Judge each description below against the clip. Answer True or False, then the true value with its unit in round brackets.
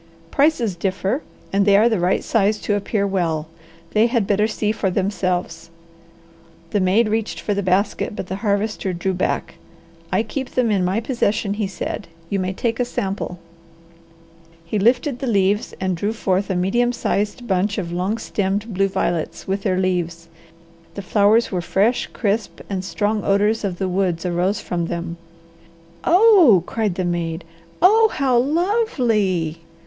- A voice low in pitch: False (200 Hz)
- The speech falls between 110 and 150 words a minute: False (165 wpm)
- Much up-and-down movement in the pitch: False (3.3 semitones)